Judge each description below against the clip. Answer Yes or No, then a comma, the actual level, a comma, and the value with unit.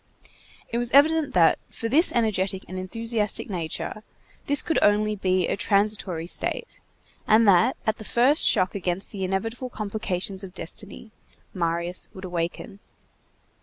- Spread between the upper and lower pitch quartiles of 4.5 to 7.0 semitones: No, average, 3.6 semitones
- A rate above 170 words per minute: No, average, 140 wpm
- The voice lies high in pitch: Yes, high, 200 Hz